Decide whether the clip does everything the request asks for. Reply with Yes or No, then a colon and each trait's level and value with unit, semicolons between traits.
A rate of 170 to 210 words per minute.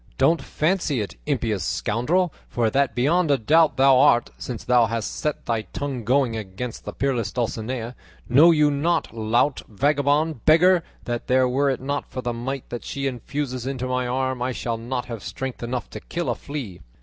Yes: average, 185 wpm